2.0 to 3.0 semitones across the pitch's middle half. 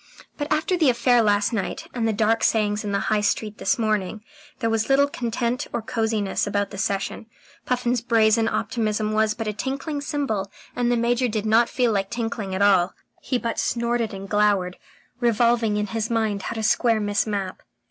Yes: narrow, 2.4 semitones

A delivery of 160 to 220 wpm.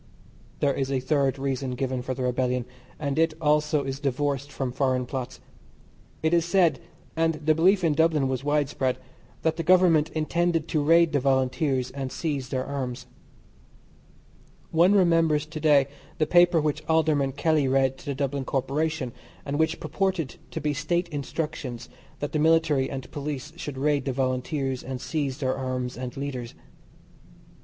Yes: average, 165 wpm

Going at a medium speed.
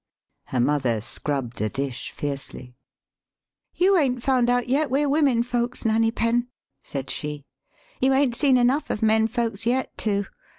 Yes: average, 175 wpm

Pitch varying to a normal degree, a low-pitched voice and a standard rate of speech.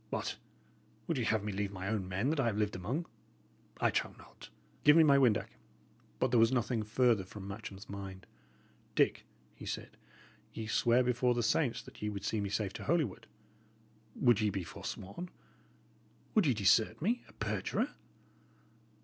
Yes: average, 4.3 semitones; low, 110 Hz; average, 175 wpm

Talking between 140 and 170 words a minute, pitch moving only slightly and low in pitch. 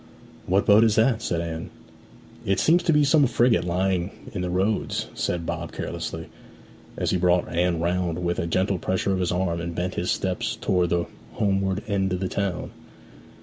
No: average, 190 wpm; narrow, 2.3 semitones; very low, 90 Hz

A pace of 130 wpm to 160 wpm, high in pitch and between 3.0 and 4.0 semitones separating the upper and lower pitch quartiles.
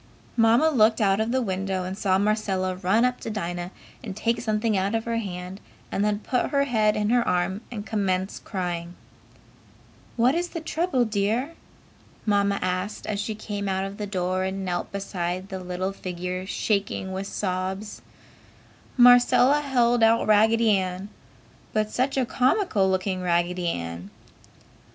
Yes: average, 155 wpm; high, 200 Hz; average, 3.5 semitones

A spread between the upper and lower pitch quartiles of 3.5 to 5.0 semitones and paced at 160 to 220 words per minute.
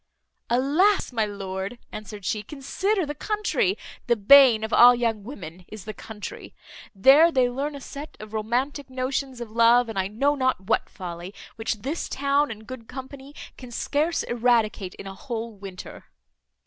Yes: average, 4.7 semitones; average, 165 wpm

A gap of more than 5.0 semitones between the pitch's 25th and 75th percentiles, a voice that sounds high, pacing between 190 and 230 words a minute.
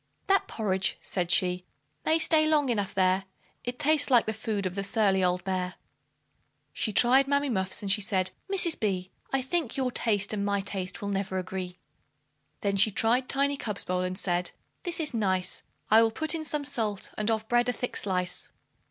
Yes: wide, 5.5 semitones; high, 210 Hz; average, 195 wpm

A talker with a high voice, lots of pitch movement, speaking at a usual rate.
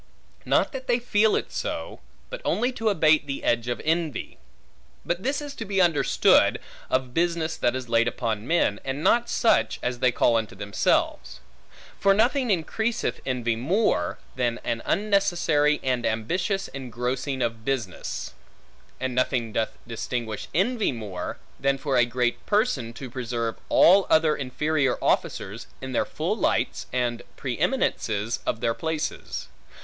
No: low, 130 Hz; wide, 7.5 semitones; average, 150 wpm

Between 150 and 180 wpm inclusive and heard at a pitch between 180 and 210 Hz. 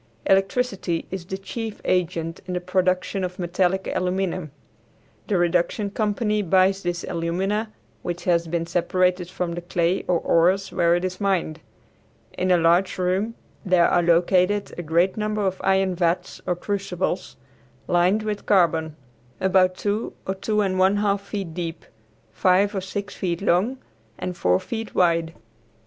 Yes: average, 155 wpm; medium, 185 Hz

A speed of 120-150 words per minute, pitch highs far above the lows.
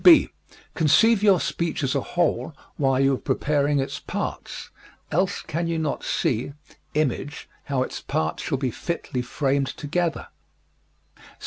No: average, 140 wpm; average, 3.9 semitones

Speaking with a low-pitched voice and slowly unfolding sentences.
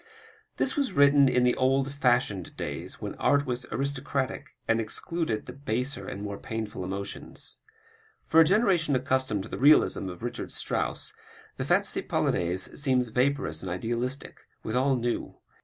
No: low, 125 Hz; average, 150 wpm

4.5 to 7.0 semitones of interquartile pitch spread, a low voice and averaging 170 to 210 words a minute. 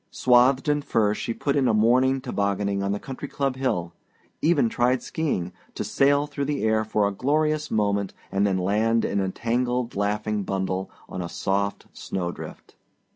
Yes: average, 4.9 semitones; low, 110 Hz; average, 180 wpm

